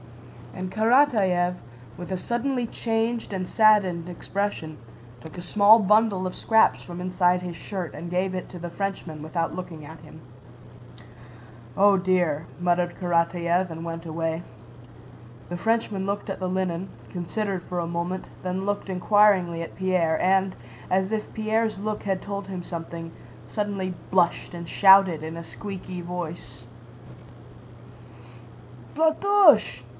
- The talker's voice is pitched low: No, medium, 185 Hz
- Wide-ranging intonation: No, average, 3.0 semitones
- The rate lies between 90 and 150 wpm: Yes, average, 140 wpm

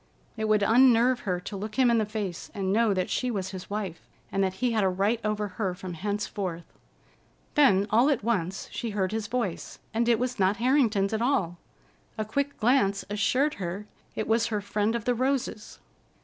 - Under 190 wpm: No, average, 200 wpm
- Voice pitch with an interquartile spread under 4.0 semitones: Yes, average, 3.3 semitones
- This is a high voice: Yes, high, 215 Hz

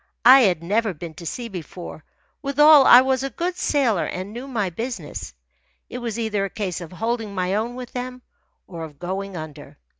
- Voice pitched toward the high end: Yes, high, 215 Hz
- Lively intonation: Yes, wide, 5.8 semitones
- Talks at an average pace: Yes, average, 190 wpm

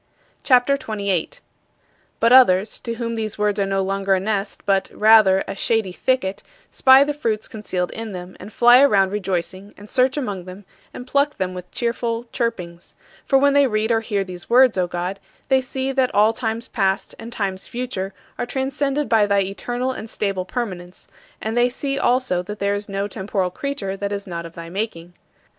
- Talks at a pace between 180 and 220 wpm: Yes, average, 190 wpm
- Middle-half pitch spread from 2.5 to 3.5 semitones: No, average, 4.3 semitones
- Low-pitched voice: No, high, 210 Hz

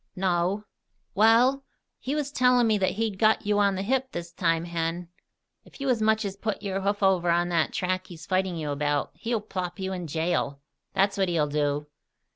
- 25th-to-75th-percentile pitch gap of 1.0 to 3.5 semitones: No, average, 4.1 semitones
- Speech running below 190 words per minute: No, average, 200 wpm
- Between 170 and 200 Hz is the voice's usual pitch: Yes, high, 190 Hz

